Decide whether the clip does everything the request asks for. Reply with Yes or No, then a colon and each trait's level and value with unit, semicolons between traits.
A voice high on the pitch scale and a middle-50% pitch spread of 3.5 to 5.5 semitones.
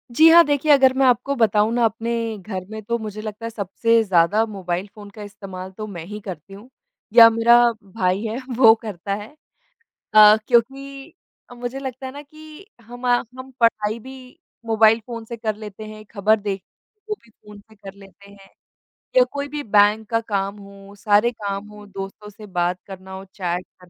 No: high, 215 Hz; average, 3.1 semitones